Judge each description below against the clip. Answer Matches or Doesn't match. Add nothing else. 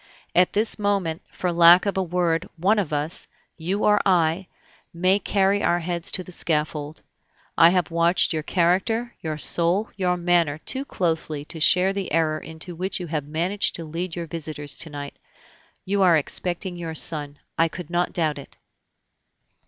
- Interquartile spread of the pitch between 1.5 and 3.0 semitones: Matches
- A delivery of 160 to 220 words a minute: Matches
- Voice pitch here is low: Doesn't match